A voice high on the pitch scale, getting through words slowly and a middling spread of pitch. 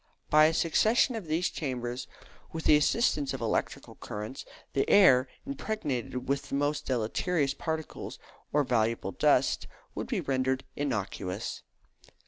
No: medium, 140 Hz; slow, 130 wpm; average, 4.1 semitones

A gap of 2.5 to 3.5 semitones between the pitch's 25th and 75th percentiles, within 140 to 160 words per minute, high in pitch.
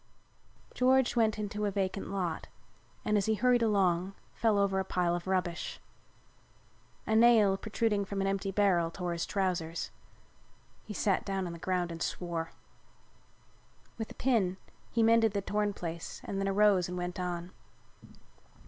Yes: average, 3.0 semitones; average, 155 wpm; high, 195 Hz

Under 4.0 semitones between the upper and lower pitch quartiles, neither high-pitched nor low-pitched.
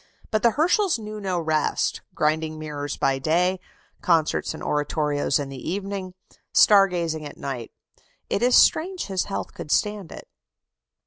No: average, 5.3 semitones; medium, 170 Hz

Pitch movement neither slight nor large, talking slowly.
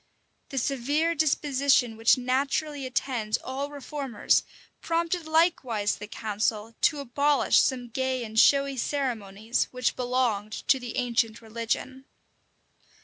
Yes: average, 3.7 semitones; slow, 115 wpm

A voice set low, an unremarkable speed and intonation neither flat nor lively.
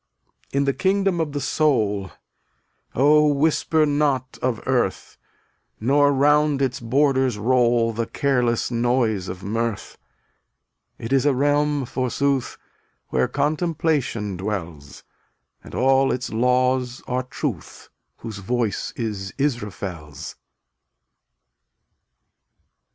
No: low, 130 Hz; slow, 100 wpm; average, 4.0 semitones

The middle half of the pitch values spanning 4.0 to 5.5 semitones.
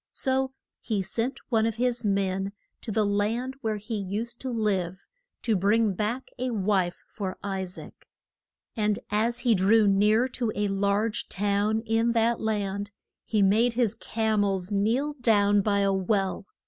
No: narrow, 2.5 semitones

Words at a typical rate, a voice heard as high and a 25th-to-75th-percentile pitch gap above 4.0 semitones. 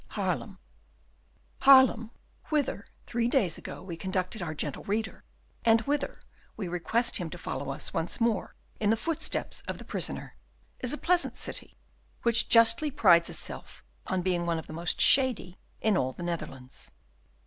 Yes: average, 160 wpm; high, 205 Hz; wide, 5.5 semitones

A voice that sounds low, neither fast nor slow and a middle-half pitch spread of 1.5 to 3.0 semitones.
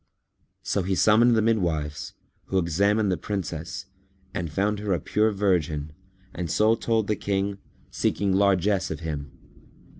No: very low, 95 Hz; average, 145 wpm; average, 3.8 semitones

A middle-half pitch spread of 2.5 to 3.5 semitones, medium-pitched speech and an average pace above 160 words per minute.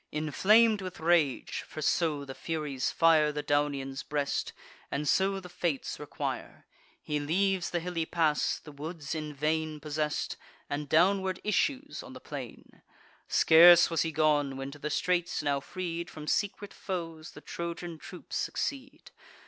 No: average, 3.2 semitones; medium, 160 Hz; average, 150 wpm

